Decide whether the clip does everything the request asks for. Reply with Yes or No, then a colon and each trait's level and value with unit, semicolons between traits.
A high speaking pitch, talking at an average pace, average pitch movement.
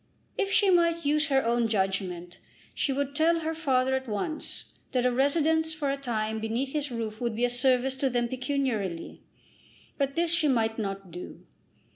Yes: very high, 260 Hz; average, 180 wpm; average, 5.0 semitones